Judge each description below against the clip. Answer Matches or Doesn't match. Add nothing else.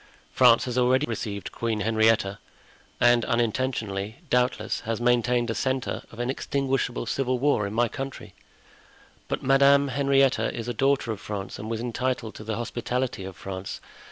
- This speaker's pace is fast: Doesn't match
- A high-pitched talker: Doesn't match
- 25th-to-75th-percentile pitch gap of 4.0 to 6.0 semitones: Doesn't match